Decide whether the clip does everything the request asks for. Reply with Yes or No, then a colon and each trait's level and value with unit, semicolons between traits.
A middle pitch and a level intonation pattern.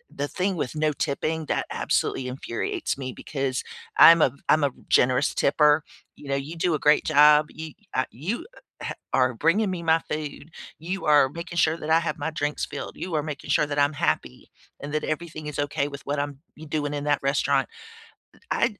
Yes: medium, 150 Hz; narrow, 2.1 semitones